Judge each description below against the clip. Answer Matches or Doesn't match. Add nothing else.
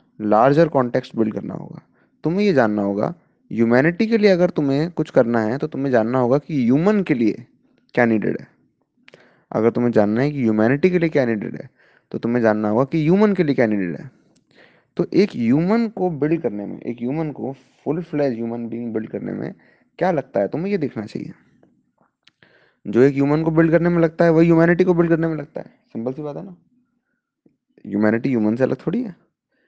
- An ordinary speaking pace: Doesn't match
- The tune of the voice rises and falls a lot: Matches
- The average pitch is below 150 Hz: Matches